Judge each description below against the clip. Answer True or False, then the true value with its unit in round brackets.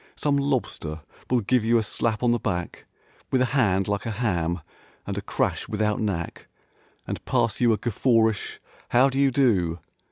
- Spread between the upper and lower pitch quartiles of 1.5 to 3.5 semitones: False (4.2 semitones)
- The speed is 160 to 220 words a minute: True (180 wpm)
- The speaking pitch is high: False (110 Hz)